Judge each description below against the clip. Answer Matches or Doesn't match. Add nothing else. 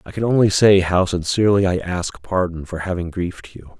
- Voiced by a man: Matches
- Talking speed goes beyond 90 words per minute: Matches